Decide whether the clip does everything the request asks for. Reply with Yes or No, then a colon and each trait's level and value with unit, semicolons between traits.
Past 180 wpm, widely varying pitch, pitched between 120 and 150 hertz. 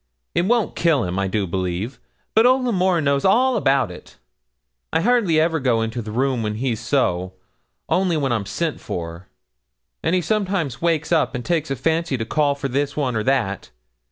Yes: average, 190 wpm; wide, 7.1 semitones; medium, 140 Hz